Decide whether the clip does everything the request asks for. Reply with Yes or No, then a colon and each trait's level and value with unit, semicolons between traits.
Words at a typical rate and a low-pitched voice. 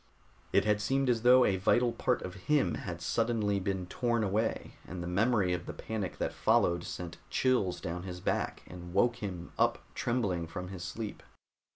Yes: average, 185 wpm; low, 100 Hz